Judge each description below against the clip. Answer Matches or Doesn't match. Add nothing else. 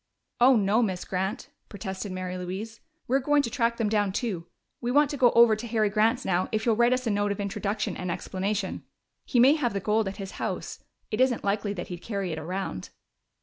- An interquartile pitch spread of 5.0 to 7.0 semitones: Doesn't match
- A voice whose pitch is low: Doesn't match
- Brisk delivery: Matches